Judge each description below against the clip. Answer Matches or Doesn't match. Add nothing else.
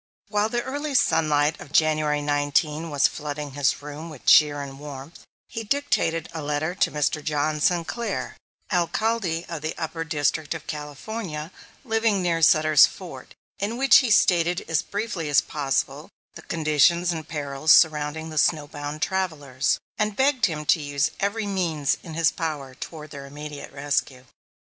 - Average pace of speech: Matches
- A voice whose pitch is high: Doesn't match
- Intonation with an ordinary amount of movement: Matches